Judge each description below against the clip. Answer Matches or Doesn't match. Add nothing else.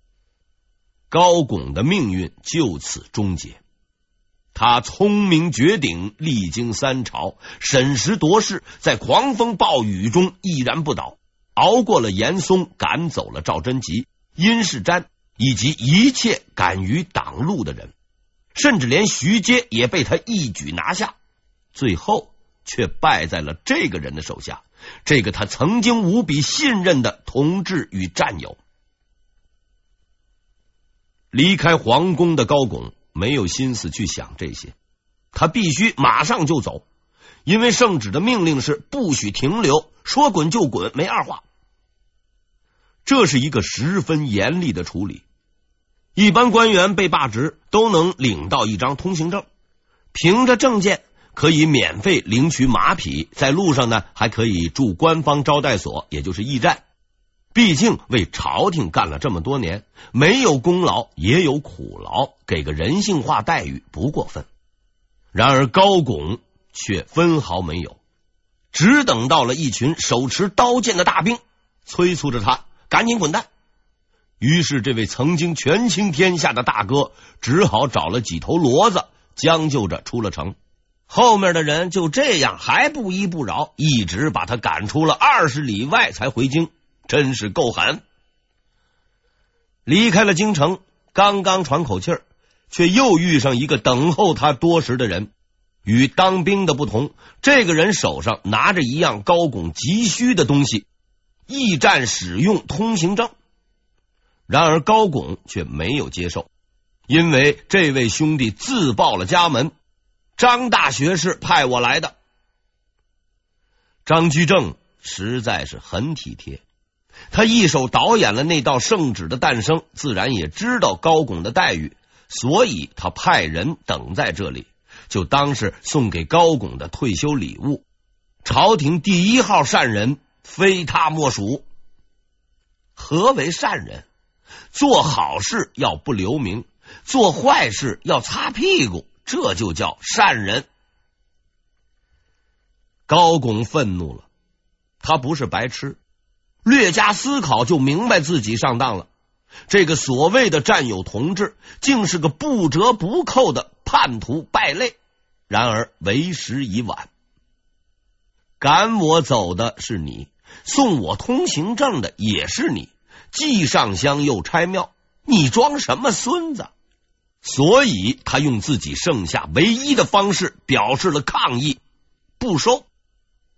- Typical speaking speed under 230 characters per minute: Matches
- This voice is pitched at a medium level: Matches